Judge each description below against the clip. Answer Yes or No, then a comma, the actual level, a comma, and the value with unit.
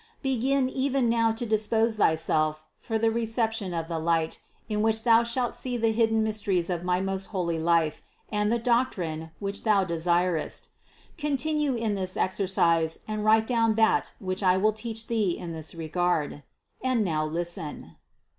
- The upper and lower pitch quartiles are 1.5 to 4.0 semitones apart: No, average, 4.9 semitones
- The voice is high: Yes, high, 210 Hz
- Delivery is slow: No, average, 165 wpm